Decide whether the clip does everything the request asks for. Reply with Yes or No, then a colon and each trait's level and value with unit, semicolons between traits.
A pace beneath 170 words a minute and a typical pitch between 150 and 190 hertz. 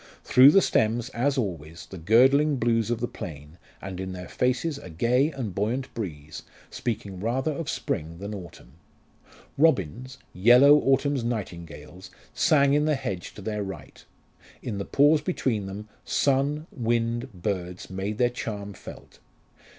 No: average, 150 wpm; low, 115 Hz